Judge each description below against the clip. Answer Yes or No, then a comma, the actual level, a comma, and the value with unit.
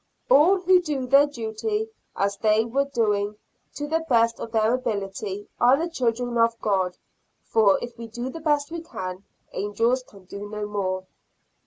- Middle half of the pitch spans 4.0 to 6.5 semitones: Yes, average, 5.2 semitones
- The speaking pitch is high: Yes, high, 230 Hz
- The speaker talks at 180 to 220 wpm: No, average, 170 wpm